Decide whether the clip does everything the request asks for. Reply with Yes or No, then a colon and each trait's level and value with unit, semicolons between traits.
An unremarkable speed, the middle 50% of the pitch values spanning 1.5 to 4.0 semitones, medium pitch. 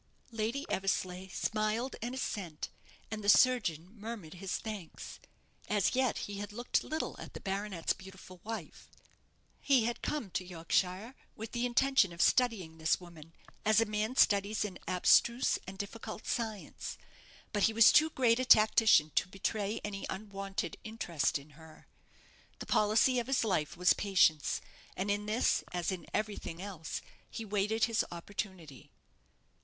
No: average, 150 wpm; average, 3.6 semitones; high, 205 Hz